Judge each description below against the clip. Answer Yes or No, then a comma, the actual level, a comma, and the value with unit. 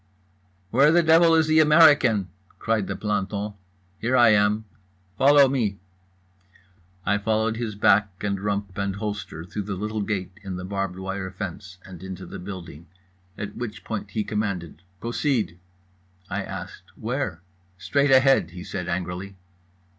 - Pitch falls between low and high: No, low, 105 Hz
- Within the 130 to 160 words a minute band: Yes, average, 145 wpm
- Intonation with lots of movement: No, average, 3.5 semitones